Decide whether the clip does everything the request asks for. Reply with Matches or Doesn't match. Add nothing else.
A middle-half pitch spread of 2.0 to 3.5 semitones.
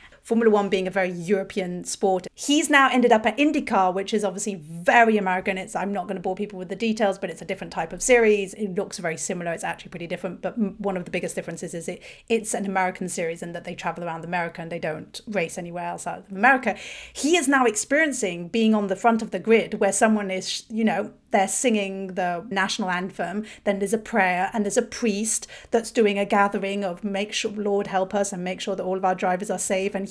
Matches